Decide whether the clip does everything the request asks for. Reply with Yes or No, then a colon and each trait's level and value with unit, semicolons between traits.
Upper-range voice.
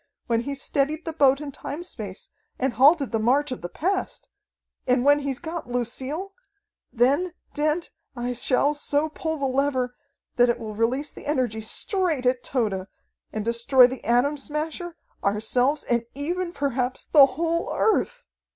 Yes: very high, 275 Hz